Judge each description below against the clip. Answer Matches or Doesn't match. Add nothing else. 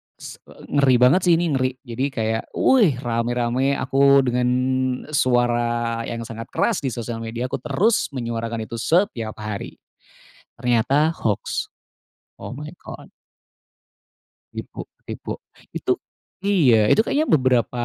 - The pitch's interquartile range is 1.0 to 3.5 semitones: Matches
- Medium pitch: Doesn't match